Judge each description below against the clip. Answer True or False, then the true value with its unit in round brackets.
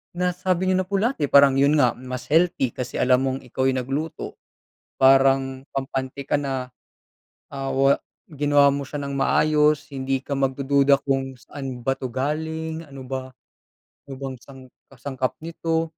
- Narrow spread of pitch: True (2.1 semitones)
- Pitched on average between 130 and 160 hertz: True (135 Hz)